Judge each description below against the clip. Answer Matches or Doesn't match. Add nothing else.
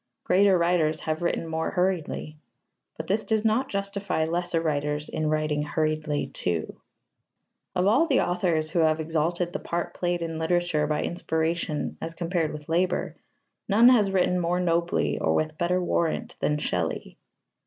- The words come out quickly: Doesn't match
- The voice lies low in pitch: Doesn't match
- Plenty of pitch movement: Doesn't match